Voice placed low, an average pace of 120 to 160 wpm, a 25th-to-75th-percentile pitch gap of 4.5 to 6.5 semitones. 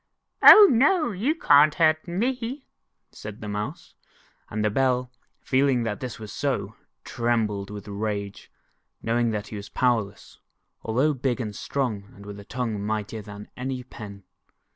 Yes: low, 115 Hz; average, 150 wpm; average, 5.2 semitones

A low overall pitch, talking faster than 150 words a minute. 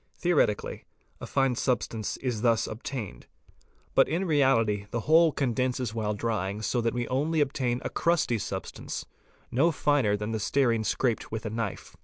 Yes: low, 120 Hz; average, 170 wpm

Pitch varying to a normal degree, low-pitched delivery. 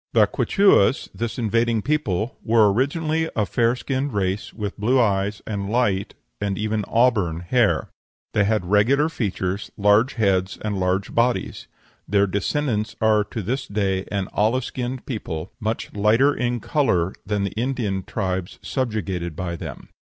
Yes: average, 3.7 semitones; low, 105 Hz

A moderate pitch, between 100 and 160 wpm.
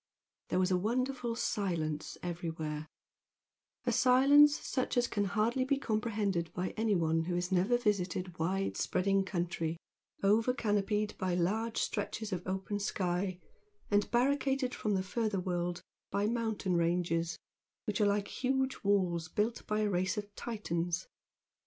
No: high, 200 Hz; average, 140 wpm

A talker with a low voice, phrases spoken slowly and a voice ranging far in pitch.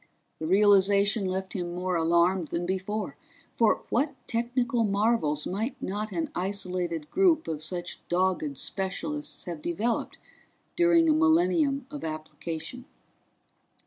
No: high, 195 Hz; slow, 120 wpm; wide, 5.9 semitones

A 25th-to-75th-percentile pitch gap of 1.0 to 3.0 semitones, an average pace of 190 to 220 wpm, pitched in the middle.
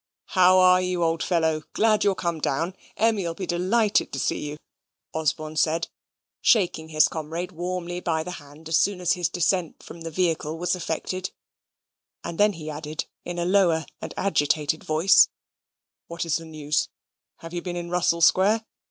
No: narrow, 2.4 semitones; average, 170 wpm; medium, 170 Hz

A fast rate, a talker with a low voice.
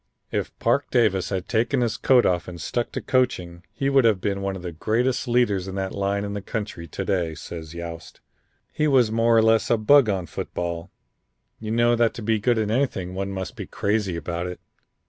Yes: fast, 220 wpm; low, 100 Hz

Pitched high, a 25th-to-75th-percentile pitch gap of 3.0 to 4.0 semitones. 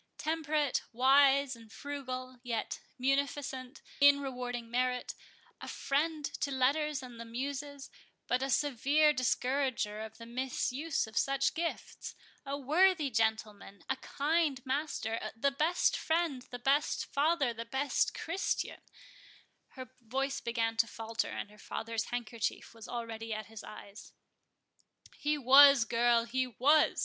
Yes: very high, 260 Hz; average, 3.5 semitones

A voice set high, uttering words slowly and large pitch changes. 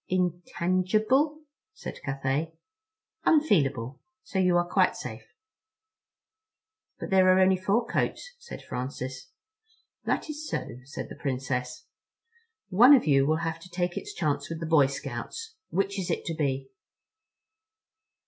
No: medium, 175 Hz; slow, 130 wpm; wide, 6.2 semitones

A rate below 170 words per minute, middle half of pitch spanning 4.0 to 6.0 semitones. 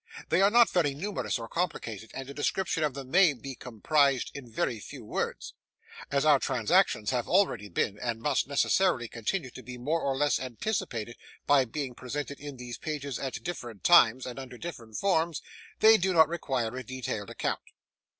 No: average, 180 wpm; average, 5.0 semitones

